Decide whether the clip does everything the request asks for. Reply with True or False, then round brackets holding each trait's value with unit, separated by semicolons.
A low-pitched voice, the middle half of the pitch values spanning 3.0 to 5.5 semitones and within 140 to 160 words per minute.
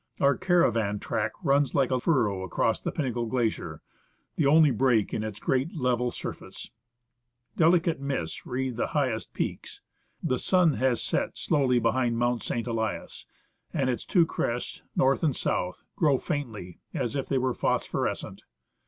True (130 Hz; 3.5 semitones; 155 wpm)